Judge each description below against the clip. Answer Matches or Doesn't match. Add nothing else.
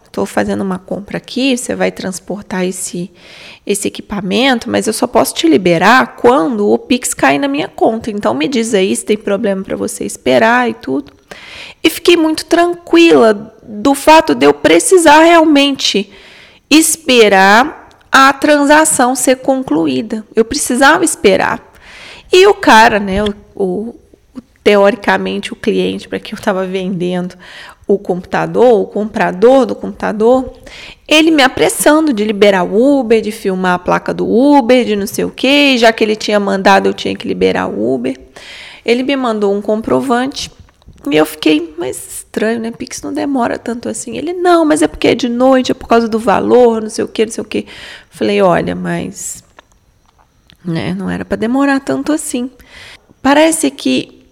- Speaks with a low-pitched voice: Doesn't match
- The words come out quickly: Doesn't match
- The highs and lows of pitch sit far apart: Matches